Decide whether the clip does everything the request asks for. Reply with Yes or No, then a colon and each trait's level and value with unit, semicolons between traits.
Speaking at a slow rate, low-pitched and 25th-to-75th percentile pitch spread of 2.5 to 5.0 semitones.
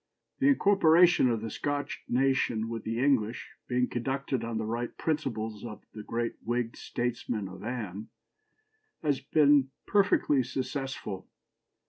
Yes: slow, 130 wpm; low, 125 Hz; average, 3.9 semitones